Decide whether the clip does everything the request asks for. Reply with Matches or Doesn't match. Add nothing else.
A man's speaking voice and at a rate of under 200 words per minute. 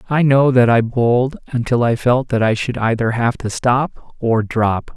Doesn't match